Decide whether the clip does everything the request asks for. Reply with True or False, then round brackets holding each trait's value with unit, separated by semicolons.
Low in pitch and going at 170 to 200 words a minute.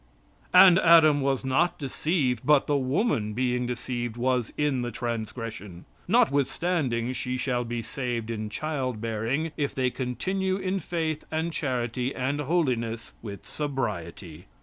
False (130 Hz; 135 wpm)